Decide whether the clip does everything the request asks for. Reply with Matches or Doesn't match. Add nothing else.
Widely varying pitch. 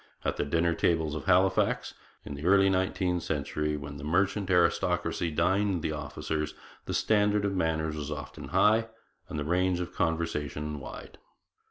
Doesn't match